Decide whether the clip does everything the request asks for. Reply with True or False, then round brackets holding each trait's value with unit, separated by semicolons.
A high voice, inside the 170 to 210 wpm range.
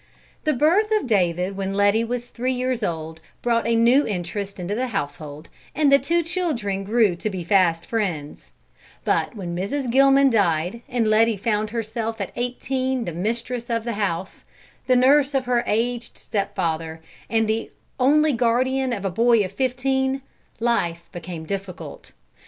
False (225 Hz; 160 wpm)